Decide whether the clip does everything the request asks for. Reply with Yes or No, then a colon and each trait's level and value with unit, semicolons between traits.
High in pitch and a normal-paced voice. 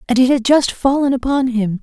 No: very high, 255 Hz; fast, 230 wpm